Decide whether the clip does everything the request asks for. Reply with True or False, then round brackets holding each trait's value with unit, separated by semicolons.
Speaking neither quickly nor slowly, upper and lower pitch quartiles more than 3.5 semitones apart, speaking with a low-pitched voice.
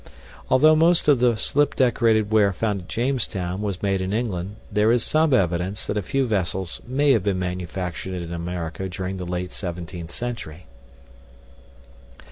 True (160 wpm; 4.8 semitones; 100 Hz)